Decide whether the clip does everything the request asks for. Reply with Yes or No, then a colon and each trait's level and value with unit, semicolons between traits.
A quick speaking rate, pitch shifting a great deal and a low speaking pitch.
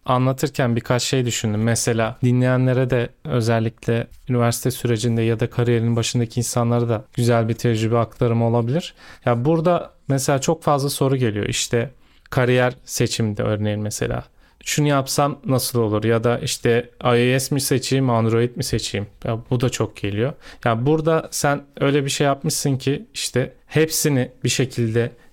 No: fast, 150 wpm; narrow, 2.6 semitones; low, 120 Hz